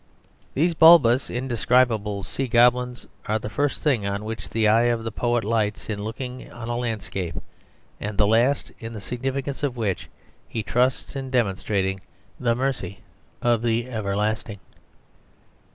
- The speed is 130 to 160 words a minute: Yes, average, 150 wpm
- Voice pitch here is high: No, low, 115 Hz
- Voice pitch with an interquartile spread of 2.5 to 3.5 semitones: Yes, average, 3.0 semitones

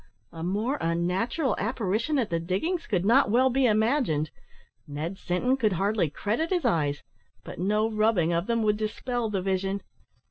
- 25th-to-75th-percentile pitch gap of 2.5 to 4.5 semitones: No, average, 5.1 semitones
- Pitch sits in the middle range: No, high, 210 Hz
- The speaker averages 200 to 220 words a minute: No, average, 165 wpm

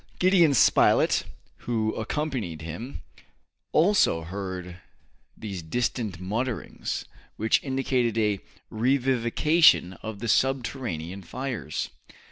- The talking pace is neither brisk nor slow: No, slow, 90 wpm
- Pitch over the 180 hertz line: No, low, 115 Hz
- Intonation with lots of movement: Yes, wide, 5.9 semitones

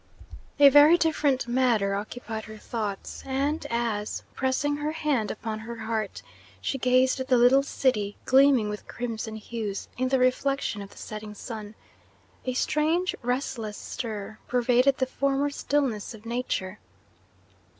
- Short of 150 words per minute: Yes, average, 140 wpm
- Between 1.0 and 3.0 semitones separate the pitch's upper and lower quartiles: No, average, 4.0 semitones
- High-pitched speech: Yes, high, 245 Hz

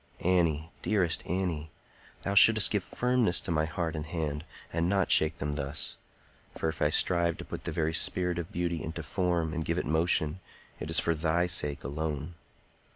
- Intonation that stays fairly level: Yes, narrow, 2.2 semitones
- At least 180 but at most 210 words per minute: Yes, average, 185 wpm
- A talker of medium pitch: No, very low, 80 Hz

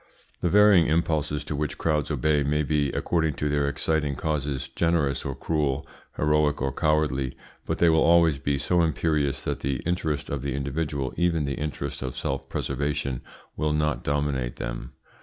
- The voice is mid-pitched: No, very low, 75 Hz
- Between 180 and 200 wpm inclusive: No, average, 170 wpm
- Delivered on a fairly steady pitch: Yes, narrow, 2.2 semitones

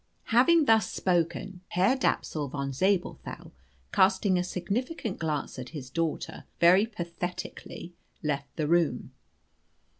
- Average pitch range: Yes, average, 4.1 semitones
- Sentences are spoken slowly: Yes, slow, 115 wpm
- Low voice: No, medium, 175 Hz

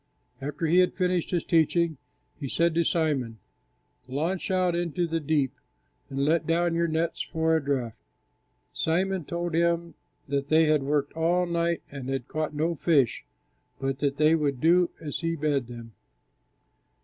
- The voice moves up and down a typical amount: Yes, average, 3.2 semitones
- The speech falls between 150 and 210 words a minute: Yes, average, 160 wpm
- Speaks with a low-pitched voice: No, medium, 160 Hz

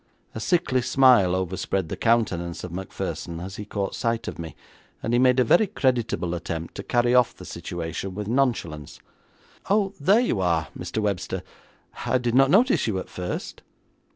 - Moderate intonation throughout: No, wide, 6.2 semitones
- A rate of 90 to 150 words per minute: No, average, 175 wpm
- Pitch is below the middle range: Yes, low, 110 Hz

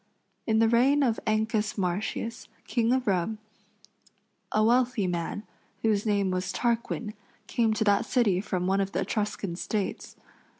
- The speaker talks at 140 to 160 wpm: Yes, average, 145 wpm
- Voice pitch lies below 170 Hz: No, high, 215 Hz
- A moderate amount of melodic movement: Yes, average, 3.0 semitones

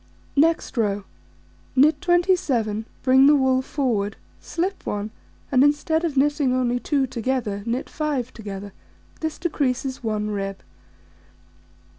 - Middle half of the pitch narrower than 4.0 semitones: No, average, 5.2 semitones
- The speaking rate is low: Yes, slow, 120 wpm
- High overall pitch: Yes, very high, 260 Hz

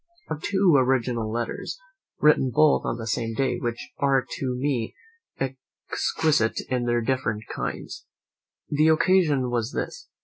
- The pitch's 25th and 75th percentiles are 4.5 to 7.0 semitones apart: No, average, 3.7 semitones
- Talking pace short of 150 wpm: Yes, average, 140 wpm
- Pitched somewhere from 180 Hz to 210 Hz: No, low, 130 Hz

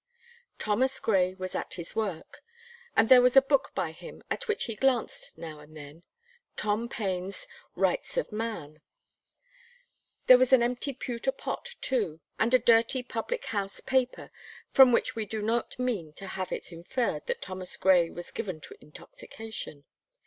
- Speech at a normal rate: Yes, average, 165 wpm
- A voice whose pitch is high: Yes, high, 220 Hz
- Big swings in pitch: Yes, wide, 5.7 semitones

